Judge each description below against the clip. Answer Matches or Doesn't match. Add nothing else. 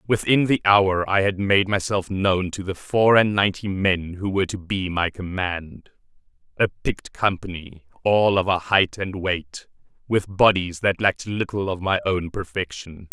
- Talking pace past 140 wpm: Matches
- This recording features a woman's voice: Doesn't match